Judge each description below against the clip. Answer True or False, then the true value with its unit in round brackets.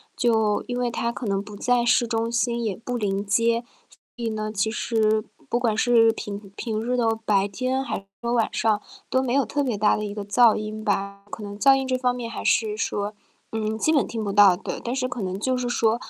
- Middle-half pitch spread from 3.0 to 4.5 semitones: False (2.6 semitones)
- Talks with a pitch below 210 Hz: False (225 Hz)